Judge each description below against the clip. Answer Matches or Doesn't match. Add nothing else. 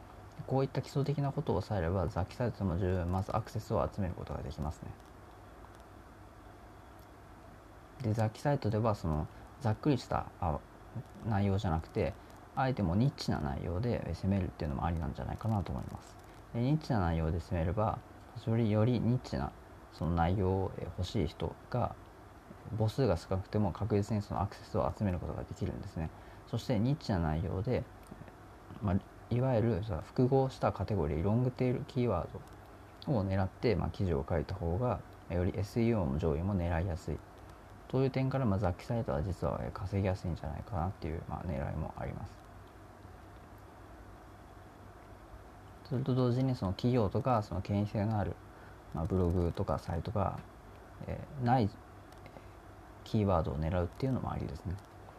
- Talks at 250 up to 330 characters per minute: Doesn't match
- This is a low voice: Matches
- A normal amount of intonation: Matches